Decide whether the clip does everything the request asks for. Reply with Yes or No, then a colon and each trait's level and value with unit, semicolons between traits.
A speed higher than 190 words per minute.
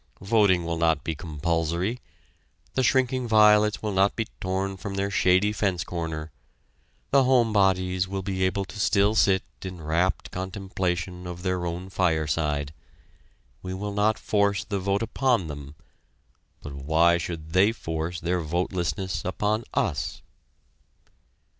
No: average, 140 wpm